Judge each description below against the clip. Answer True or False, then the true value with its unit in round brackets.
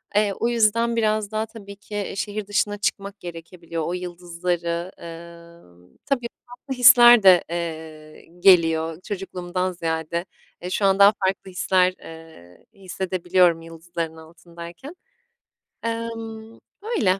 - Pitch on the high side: False (180 Hz)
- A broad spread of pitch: False (3.7 semitones)